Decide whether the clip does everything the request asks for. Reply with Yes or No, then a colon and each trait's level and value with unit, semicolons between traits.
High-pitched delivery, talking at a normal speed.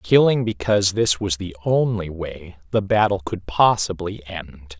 No: very low, 95 Hz; average, 150 wpm